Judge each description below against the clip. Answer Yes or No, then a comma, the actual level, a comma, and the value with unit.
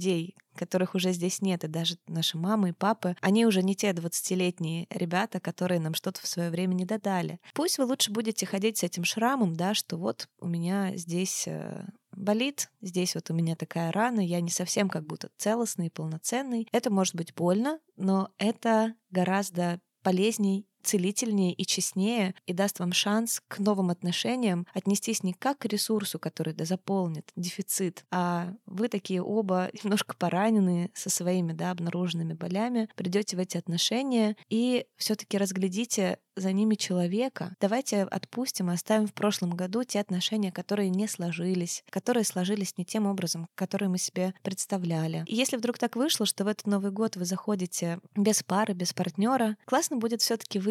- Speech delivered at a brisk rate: Yes, fast, 165 wpm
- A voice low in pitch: No, high, 190 Hz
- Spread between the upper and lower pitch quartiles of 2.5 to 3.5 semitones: Yes, average, 3.2 semitones